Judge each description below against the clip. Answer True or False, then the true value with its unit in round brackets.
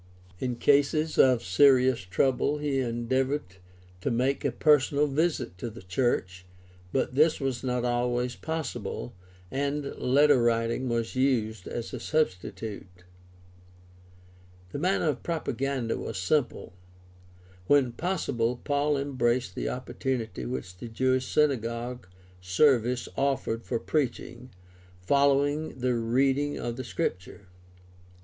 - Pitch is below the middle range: True (125 Hz)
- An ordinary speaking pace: False (115 wpm)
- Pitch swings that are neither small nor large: True (3.3 semitones)